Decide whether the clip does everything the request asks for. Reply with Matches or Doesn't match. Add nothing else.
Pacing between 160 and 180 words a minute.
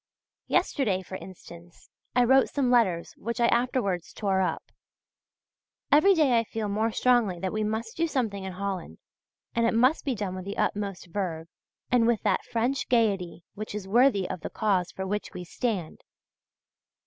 Matches